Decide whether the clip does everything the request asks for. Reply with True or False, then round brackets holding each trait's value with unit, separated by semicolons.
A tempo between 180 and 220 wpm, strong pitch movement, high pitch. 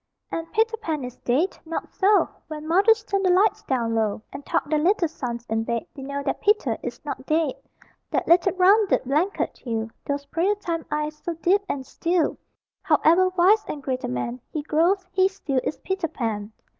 True (195 wpm; 6.1 semitones; 320 Hz)